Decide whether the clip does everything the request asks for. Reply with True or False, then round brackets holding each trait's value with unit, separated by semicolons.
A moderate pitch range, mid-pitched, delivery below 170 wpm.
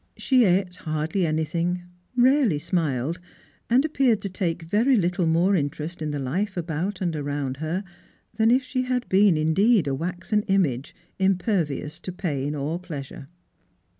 True (4.6 semitones; 175 Hz; 150 wpm)